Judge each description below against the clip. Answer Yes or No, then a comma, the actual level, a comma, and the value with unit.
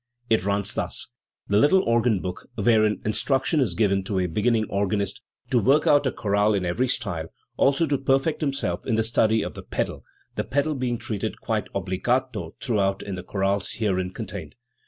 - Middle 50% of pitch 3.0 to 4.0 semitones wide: No, average, 4.7 semitones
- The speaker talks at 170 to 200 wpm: Yes, average, 185 wpm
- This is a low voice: Yes, low, 110 Hz